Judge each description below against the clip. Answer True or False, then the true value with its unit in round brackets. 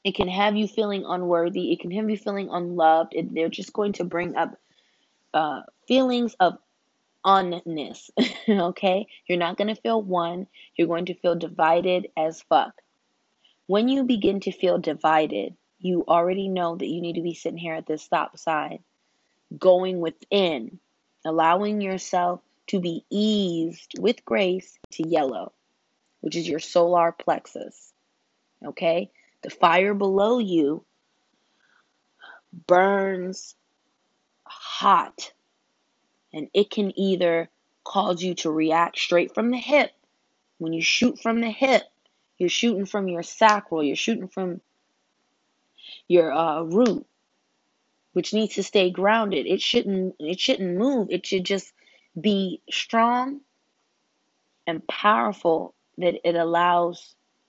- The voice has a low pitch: False (185 Hz)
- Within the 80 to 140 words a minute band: True (135 wpm)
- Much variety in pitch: False (3.5 semitones)